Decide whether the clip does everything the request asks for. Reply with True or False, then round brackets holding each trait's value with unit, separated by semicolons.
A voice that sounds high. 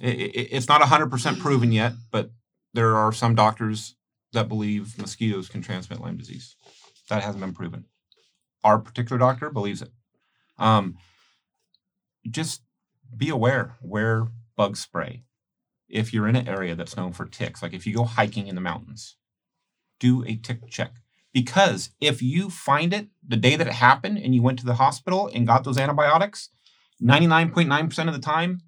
False (120 Hz)